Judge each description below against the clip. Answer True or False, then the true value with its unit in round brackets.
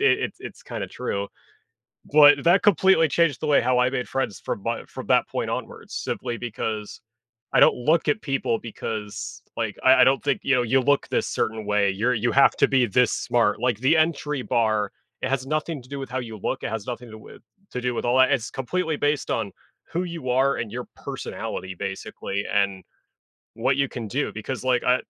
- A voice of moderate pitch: False (125 Hz)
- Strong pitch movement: False (3.8 semitones)